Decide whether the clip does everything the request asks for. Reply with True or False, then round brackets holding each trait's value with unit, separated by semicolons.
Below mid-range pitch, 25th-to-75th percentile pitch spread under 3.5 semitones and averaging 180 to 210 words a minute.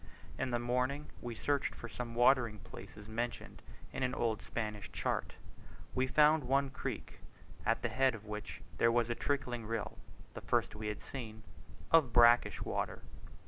False (120 Hz; 3.0 semitones; 165 wpm)